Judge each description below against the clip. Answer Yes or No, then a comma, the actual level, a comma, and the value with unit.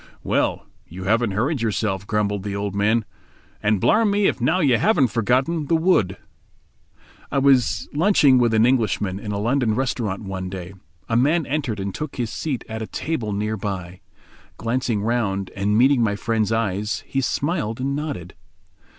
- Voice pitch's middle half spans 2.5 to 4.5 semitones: No, average, 4.9 semitones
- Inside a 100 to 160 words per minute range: No, average, 170 wpm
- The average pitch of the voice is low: Yes, low, 115 Hz